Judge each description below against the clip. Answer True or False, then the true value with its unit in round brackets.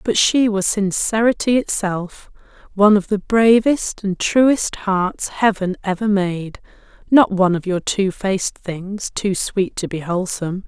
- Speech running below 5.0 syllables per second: True (4.5 syllables/s)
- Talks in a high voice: True (200 Hz)